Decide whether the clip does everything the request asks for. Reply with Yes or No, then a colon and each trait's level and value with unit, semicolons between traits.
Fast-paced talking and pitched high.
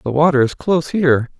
No: fast, 215 wpm; medium, 140 Hz